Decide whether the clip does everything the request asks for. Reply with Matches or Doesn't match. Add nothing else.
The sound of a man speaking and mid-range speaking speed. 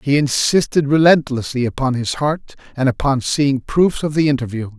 Matches